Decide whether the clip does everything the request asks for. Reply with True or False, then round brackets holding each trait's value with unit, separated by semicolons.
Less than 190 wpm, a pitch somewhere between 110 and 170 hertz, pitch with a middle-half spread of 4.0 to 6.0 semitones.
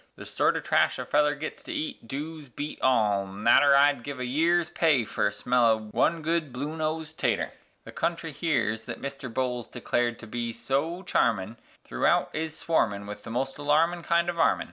False (195 wpm; 140 Hz; 5.4 semitones)